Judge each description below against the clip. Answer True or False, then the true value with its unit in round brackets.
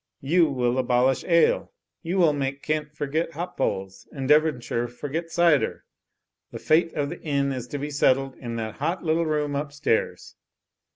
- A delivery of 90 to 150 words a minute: False (165 wpm)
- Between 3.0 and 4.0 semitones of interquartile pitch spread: True (3.4 semitones)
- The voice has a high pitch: False (145 Hz)